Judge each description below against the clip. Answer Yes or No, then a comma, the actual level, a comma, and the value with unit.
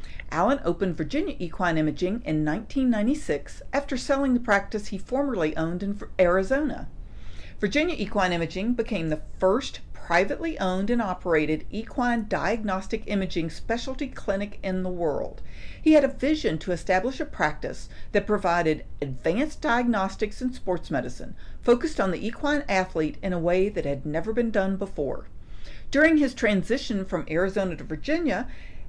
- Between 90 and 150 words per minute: Yes, average, 145 wpm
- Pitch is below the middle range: No, high, 200 Hz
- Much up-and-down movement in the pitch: Yes, wide, 6.0 semitones